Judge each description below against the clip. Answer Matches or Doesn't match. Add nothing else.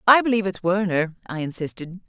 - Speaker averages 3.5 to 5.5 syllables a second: Doesn't match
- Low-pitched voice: Doesn't match